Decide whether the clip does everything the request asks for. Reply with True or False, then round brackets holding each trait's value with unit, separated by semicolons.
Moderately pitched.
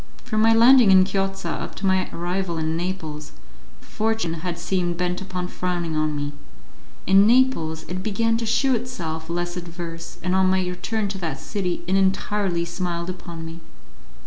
True (180 Hz)